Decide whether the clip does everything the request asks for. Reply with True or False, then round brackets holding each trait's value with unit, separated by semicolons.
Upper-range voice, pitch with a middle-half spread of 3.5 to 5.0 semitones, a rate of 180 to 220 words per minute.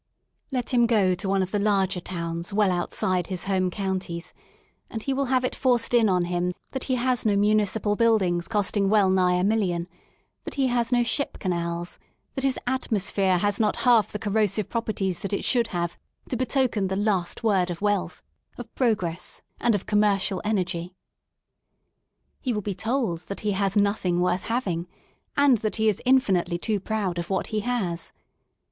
True (205 Hz; 3.8 semitones; 185 wpm)